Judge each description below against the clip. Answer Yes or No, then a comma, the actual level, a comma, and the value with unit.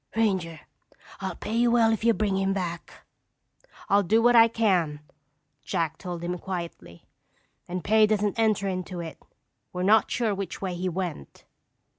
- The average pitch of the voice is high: Yes, high, 195 Hz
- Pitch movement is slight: No, average, 3.9 semitones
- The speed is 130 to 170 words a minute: Yes, average, 160 wpm